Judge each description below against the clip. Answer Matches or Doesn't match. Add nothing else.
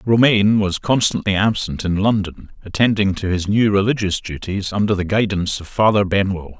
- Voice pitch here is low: Matches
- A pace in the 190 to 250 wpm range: Doesn't match